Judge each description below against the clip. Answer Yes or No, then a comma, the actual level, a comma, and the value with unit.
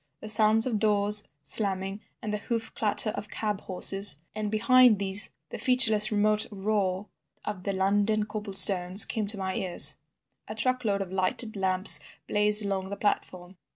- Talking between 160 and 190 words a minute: Yes, average, 165 wpm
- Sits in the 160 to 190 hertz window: No, high, 205 Hz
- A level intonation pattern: Yes, narrow, 1.9 semitones